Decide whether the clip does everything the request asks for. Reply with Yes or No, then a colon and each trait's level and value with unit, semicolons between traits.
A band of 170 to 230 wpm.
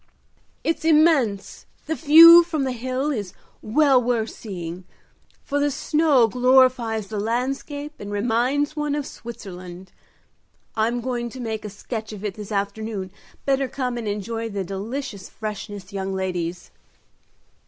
No: average, 140 wpm